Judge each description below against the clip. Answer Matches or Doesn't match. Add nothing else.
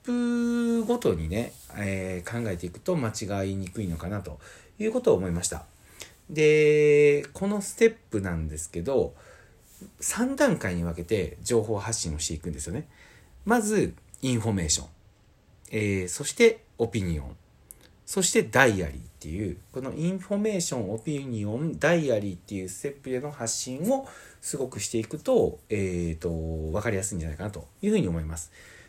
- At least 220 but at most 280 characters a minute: Doesn't match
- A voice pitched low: Matches